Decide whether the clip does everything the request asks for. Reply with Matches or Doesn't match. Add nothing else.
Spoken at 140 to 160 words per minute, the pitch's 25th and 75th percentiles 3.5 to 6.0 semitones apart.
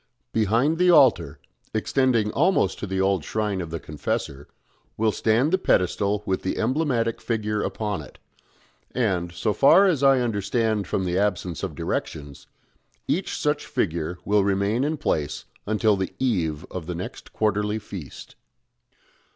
Matches